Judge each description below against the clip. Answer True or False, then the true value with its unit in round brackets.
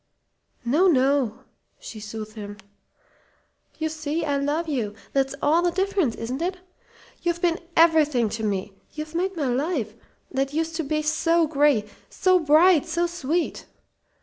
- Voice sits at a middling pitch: False (300 Hz)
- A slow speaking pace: False (150 wpm)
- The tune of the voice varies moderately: True (4.7 semitones)